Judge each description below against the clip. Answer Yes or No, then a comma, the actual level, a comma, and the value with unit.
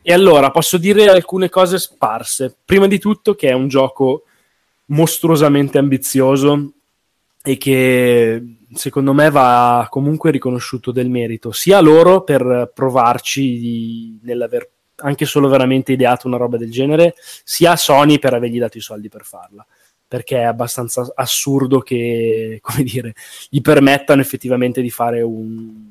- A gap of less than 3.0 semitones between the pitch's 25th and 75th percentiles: No, average, 3.7 semitones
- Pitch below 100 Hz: No, low, 130 Hz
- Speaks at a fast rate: No, average, 145 wpm